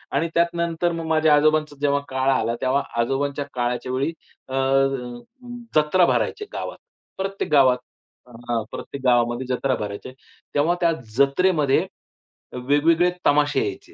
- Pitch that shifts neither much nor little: Yes, average, 4.3 semitones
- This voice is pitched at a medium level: Yes, medium, 145 Hz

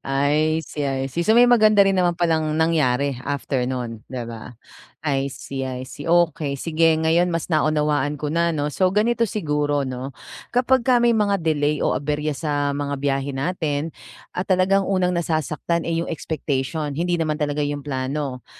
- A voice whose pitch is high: No, medium, 150 Hz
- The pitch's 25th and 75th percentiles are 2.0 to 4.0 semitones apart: Yes, average, 3.4 semitones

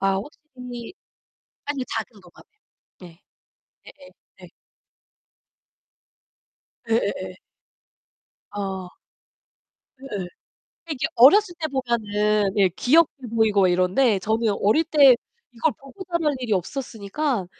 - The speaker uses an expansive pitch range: Yes, wide, 5.7 semitones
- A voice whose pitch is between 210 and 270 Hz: Yes, high, 230 Hz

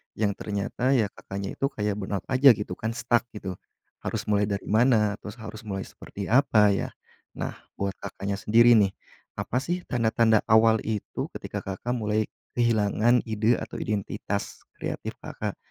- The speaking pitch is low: Yes, low, 110 Hz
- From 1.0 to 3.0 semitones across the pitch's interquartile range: Yes, narrow, 2.6 semitones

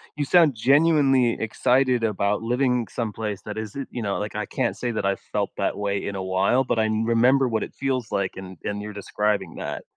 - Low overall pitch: Yes, low, 110 Hz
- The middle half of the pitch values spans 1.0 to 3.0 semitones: No, average, 3.8 semitones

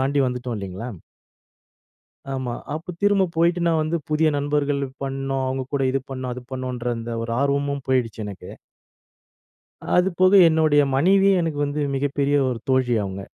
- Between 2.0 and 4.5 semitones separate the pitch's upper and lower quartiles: Yes, average, 3.7 semitones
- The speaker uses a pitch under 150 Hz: Yes, medium, 140 Hz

